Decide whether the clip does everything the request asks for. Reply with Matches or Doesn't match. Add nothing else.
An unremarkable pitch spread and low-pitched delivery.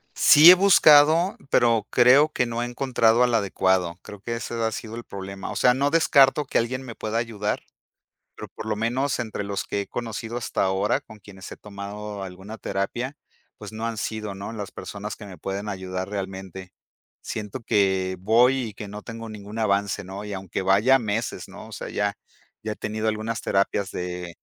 Matches